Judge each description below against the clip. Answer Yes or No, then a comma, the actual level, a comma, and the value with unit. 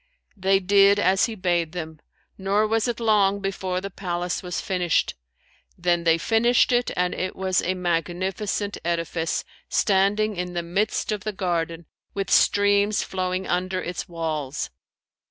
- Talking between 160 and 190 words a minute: No, average, 150 wpm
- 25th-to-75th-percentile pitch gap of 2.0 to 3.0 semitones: Yes, narrow, 2.6 semitones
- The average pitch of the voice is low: No, medium, 185 Hz